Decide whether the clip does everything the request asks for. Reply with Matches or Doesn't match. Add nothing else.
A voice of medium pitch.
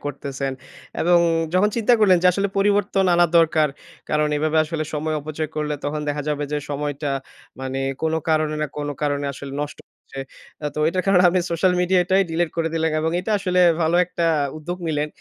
Matches